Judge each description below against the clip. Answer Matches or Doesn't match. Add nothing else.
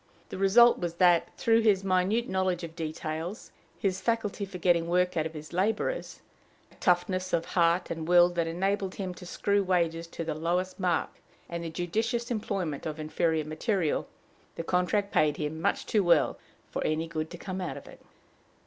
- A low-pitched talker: Doesn't match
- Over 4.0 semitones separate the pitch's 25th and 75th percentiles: Doesn't match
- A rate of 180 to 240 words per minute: Matches